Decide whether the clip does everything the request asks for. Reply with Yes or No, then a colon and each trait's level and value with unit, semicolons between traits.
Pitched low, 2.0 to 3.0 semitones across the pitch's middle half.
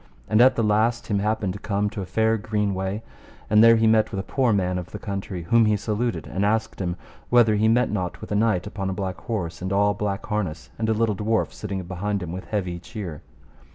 Yes: low, 105 Hz; average, 2.7 semitones